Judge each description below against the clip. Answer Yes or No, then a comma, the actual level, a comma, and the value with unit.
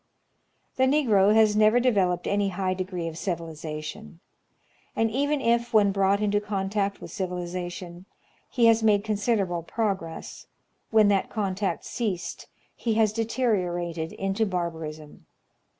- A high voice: Yes, high, 200 Hz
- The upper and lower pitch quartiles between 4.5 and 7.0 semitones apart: No, average, 3.7 semitones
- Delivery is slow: Yes, slow, 130 wpm